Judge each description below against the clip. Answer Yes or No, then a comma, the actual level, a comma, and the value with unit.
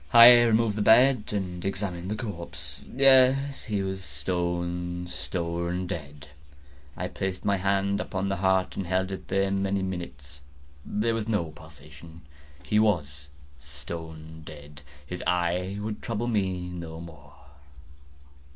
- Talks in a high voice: No, very low, 95 Hz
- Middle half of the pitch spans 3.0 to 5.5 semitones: Yes, average, 3.5 semitones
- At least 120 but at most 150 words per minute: Yes, slow, 135 wpm